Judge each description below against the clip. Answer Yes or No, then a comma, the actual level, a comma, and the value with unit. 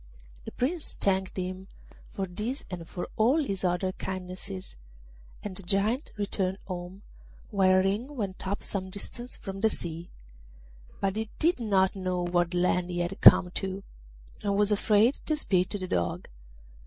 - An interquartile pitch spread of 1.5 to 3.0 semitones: Yes, narrow, 2.4 semitones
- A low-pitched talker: No, high, 190 Hz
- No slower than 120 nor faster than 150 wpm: No, average, 160 wpm